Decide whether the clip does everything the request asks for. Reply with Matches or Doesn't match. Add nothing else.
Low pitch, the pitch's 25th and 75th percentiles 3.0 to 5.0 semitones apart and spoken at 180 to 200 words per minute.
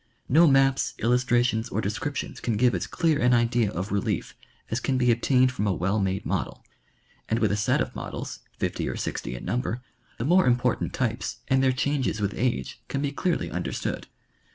Matches